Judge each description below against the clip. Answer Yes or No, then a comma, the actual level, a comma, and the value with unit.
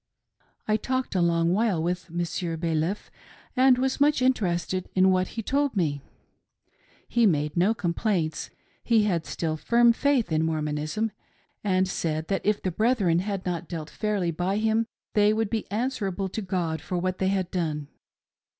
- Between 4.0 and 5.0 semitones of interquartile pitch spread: Yes, average, 4.6 semitones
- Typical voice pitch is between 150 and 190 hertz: Yes, medium, 185 Hz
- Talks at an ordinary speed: Yes, average, 165 wpm